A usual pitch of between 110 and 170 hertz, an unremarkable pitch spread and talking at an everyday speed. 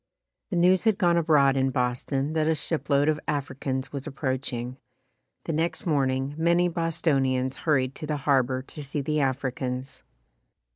Yes: medium, 140 Hz; average, 3.2 semitones; average, 150 wpm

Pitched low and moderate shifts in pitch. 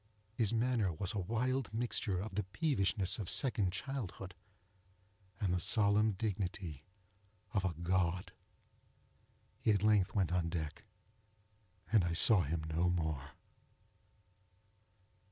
Yes: very low, 95 Hz; average, 3.7 semitones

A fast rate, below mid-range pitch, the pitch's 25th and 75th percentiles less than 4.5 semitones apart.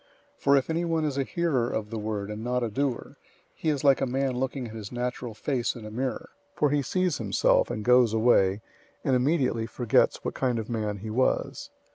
Yes: fast, 220 wpm; low, 125 Hz; average, 3.7 semitones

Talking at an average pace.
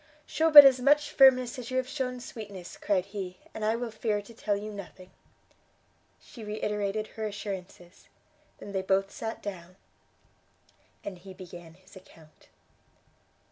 Yes: average, 150 wpm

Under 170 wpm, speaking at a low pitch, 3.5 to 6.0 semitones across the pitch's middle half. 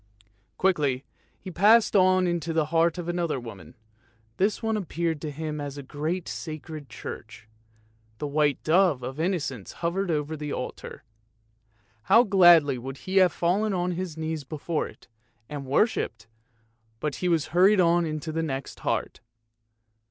No: average, 150 wpm; medium, 160 Hz; average, 3.8 semitones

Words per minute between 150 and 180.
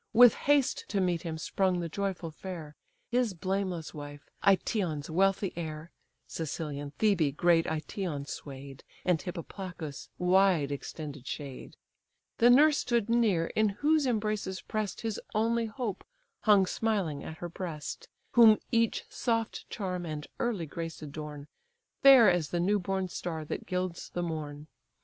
No: average, 140 wpm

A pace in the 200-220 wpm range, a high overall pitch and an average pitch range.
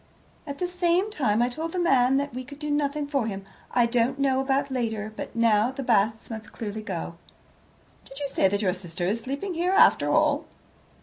Yes: fast, 205 wpm; very high, 255 Hz; average, 4.8 semitones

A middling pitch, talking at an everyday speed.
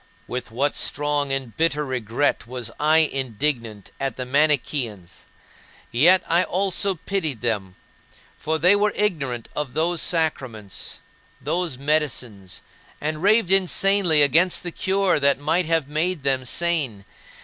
No: medium, 150 Hz; slow, 130 wpm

